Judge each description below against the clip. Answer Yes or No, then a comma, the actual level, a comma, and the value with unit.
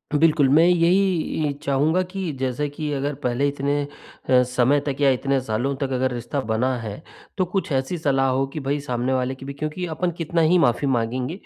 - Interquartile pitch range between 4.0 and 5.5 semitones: No, average, 3.3 semitones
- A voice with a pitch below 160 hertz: Yes, medium, 140 Hz